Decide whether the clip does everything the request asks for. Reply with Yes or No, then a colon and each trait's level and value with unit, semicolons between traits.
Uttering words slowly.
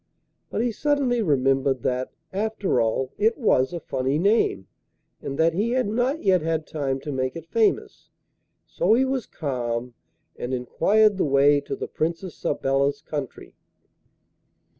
No: average, 150 wpm